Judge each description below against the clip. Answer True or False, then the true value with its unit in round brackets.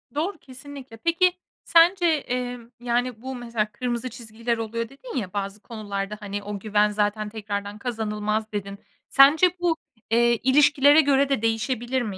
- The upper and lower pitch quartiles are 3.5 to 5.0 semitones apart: True (4.4 semitones)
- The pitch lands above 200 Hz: True (235 Hz)